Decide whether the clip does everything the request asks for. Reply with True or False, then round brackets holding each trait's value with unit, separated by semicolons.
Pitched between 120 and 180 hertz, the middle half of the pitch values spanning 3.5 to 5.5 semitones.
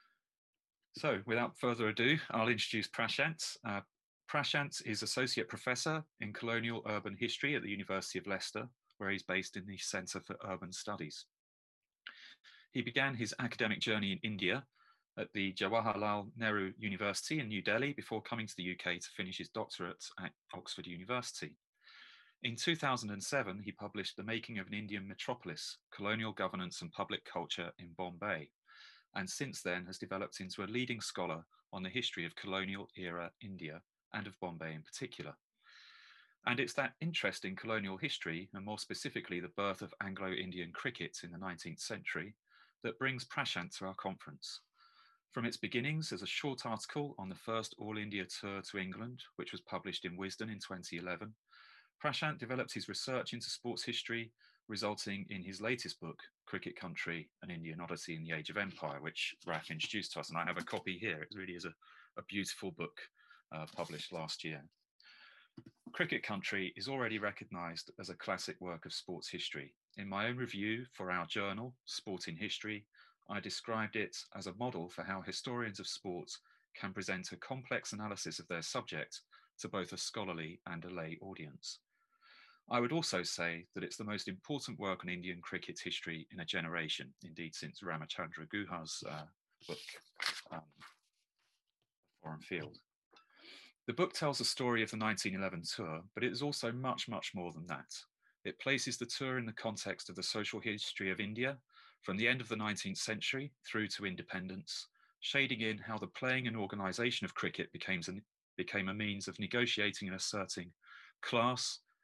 False (105 Hz; 4.1 semitones)